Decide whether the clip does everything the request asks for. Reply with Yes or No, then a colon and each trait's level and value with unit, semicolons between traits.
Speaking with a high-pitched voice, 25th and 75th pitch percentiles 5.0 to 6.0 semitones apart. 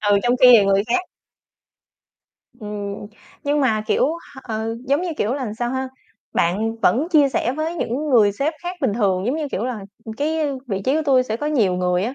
Yes: high, 240 Hz; average, 5.3 semitones